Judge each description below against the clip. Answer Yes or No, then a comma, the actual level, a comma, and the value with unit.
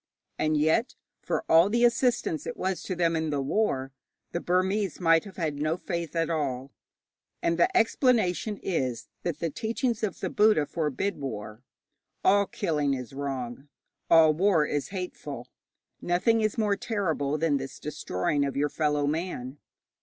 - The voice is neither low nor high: Yes, medium, 165 Hz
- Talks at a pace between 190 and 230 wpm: No, average, 160 wpm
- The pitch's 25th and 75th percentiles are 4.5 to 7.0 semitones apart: Yes, wide, 5.4 semitones